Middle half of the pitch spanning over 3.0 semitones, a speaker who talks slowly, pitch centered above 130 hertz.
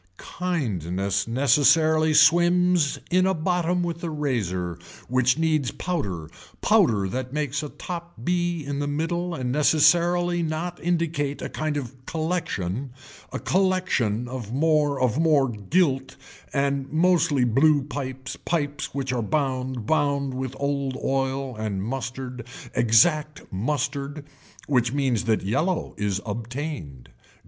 Yes: average, 4.5 semitones; slow, 125 wpm; medium, 140 Hz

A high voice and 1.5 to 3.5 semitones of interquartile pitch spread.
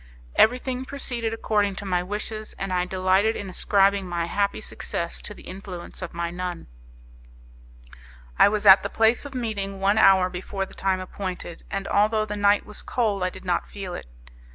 Yes: high, 195 Hz; narrow, 2.6 semitones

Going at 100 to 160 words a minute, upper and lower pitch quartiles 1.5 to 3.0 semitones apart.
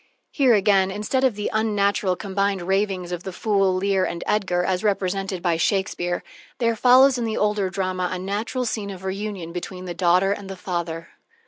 No: average, 185 wpm; narrow, 2.4 semitones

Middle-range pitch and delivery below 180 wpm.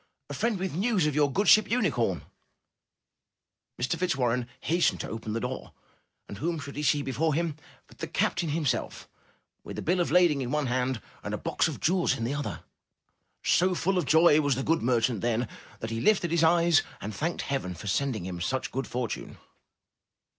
No: medium, 145 Hz; fast, 205 wpm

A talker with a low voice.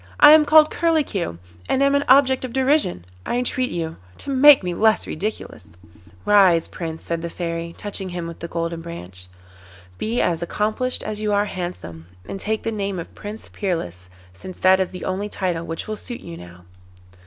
No: high, 190 Hz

